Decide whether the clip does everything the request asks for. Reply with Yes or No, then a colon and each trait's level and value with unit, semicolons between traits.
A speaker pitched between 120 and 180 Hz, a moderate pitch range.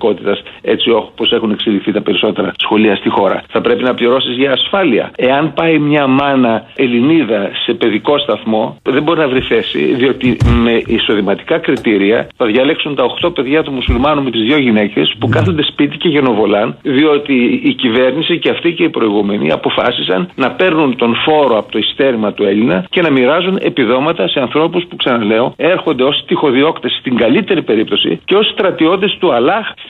Yes: low, 135 Hz; average, 4.7 semitones